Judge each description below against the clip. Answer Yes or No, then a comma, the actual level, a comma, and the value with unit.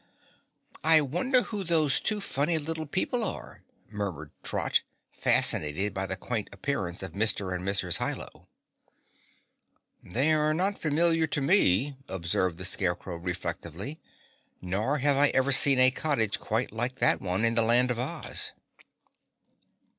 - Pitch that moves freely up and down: Yes, wide, 8.3 semitones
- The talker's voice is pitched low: Yes, low, 125 Hz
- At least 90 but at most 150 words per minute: Yes, average, 145 wpm